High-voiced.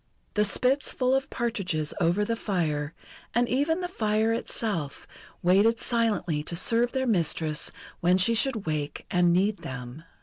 Yes: high, 205 Hz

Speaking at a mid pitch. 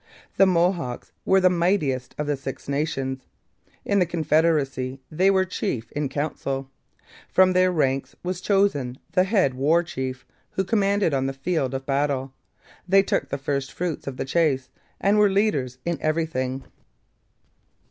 Yes: medium, 150 Hz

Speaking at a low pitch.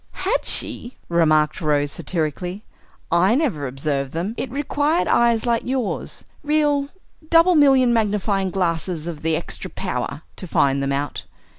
No: high, 190 Hz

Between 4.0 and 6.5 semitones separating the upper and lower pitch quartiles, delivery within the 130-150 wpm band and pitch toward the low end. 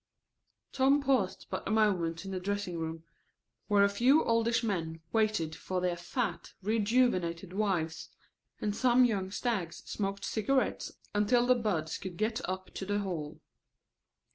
No: average, 4.3 semitones; average, 145 wpm; high, 200 Hz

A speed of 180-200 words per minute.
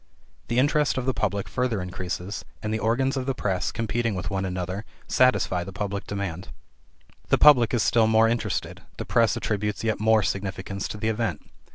Yes: average, 185 wpm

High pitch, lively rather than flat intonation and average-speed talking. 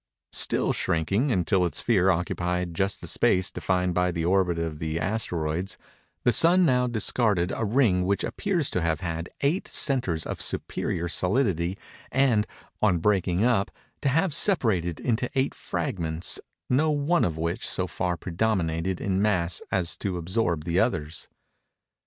No: very low, 95 Hz; wide, 5.7 semitones; average, 150 wpm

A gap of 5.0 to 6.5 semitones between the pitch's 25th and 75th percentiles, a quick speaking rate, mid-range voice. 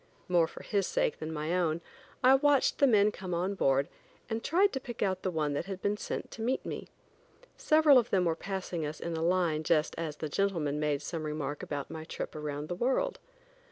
Yes: average, 5.3 semitones; fast, 220 wpm; medium, 175 Hz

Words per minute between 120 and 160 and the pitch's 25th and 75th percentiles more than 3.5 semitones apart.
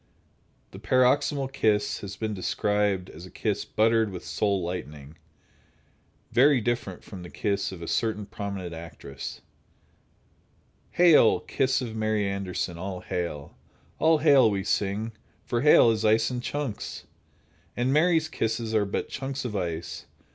Yes: average, 140 wpm; average, 4.5 semitones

